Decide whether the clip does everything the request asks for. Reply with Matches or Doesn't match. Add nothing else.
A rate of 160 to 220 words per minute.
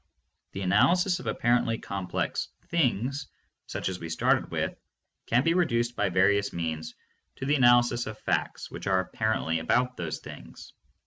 Matches